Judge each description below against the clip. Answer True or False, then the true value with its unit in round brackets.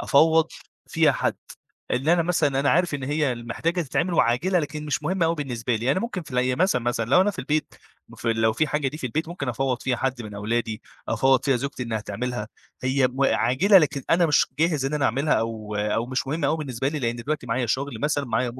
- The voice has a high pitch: False (135 Hz)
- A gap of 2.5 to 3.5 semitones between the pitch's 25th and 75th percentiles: False (4.3 semitones)